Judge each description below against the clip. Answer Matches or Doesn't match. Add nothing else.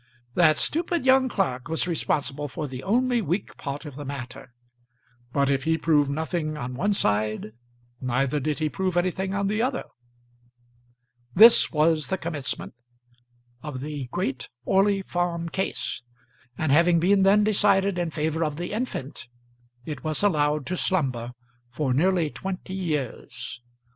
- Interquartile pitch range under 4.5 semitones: Doesn't match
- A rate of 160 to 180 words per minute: Doesn't match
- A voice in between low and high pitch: Matches